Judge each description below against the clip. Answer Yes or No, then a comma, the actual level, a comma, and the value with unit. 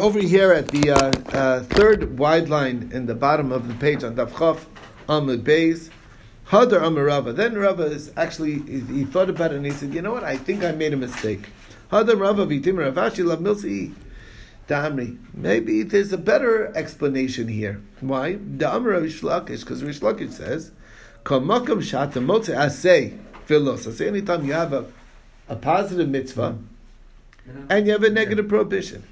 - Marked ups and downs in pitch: Yes, wide, 6.5 semitones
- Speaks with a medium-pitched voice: Yes, medium, 150 Hz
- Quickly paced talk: No, average, 160 wpm